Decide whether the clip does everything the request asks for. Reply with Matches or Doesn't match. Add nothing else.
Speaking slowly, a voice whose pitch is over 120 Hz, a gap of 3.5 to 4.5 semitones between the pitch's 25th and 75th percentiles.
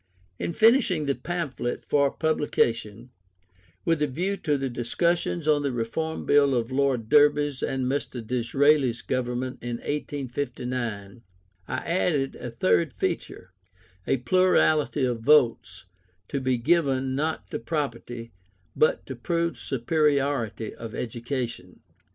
Matches